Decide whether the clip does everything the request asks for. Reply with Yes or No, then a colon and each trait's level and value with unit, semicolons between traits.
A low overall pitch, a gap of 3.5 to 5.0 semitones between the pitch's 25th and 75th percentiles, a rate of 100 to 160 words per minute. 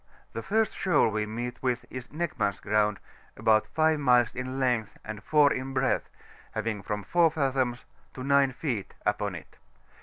No: low, 125 Hz; average, 4.3 semitones; average, 170 wpm